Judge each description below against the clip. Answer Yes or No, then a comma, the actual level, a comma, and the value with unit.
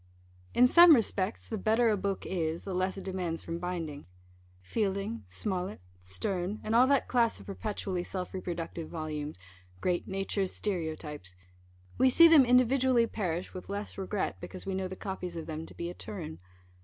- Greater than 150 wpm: Yes, average, 170 wpm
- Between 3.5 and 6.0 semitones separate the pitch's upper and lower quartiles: Yes, average, 4.3 semitones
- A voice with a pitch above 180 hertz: Yes, high, 190 Hz